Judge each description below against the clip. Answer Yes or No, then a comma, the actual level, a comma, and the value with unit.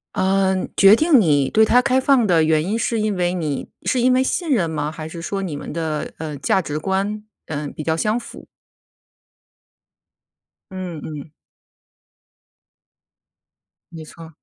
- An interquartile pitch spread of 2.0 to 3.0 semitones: No, wide, 5.5 semitones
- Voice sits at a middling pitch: Yes, medium, 180 Hz